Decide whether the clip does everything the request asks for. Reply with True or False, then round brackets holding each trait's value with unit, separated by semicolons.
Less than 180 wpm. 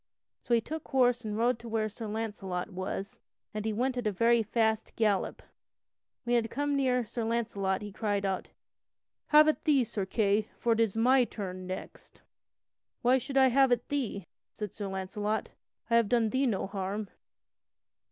False (185 wpm)